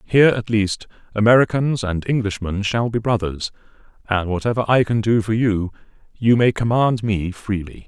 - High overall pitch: No, low, 110 Hz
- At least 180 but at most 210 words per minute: No, average, 160 wpm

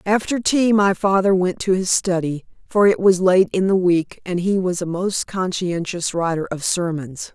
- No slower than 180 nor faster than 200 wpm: Yes, average, 195 wpm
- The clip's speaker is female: Yes, female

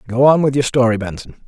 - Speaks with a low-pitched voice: Yes, low, 125 Hz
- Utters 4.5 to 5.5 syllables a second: No, 6.2 syllables/s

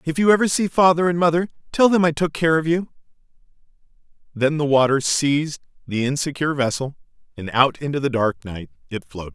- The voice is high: No, medium, 150 Hz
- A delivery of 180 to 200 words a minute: Yes, average, 185 wpm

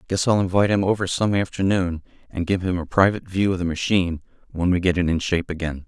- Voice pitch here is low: Yes, very low, 90 Hz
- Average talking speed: No, fast, 235 wpm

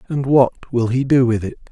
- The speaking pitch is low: Yes, low, 125 Hz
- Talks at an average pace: No, fast, 245 wpm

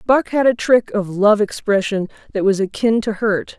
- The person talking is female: Yes, female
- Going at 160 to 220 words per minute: Yes, average, 200 wpm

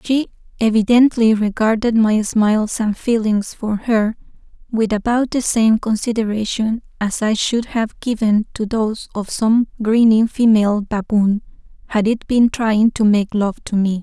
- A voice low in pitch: No, high, 220 Hz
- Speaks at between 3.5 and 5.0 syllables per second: Yes, 4.4 syllables/s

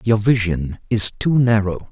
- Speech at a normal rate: Yes, average, 155 wpm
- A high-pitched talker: No, low, 105 Hz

